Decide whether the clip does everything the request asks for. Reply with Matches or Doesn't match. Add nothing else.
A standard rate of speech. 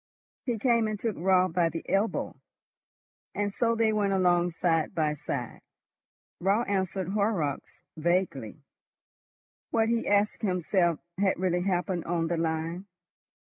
Doesn't match